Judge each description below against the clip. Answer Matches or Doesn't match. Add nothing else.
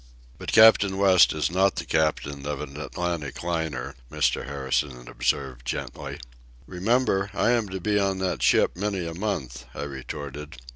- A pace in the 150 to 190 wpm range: Matches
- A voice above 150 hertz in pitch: Doesn't match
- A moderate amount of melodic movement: Doesn't match